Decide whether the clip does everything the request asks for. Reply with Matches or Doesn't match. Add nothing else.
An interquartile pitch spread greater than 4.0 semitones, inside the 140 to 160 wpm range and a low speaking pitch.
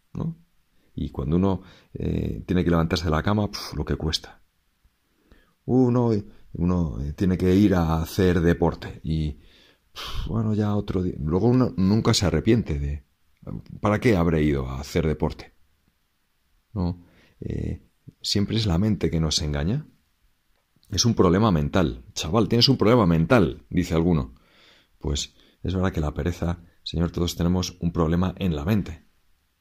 Matches